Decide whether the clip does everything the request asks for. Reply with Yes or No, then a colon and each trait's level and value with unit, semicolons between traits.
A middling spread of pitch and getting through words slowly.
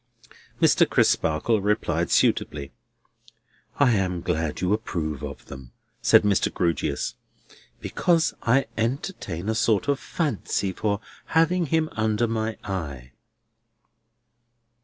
No: wide, 5.8 semitones; slow, 110 wpm